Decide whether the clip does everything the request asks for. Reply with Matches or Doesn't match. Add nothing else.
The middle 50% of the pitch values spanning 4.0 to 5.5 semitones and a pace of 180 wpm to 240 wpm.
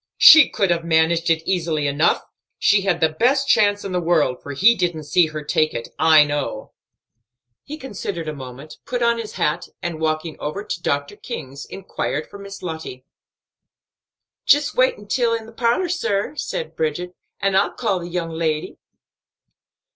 Doesn't match